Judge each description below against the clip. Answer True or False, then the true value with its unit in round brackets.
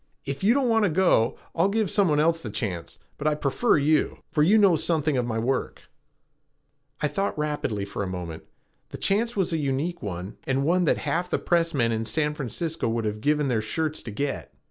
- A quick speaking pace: True (215 wpm)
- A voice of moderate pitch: True (150 Hz)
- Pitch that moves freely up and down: True (6.8 semitones)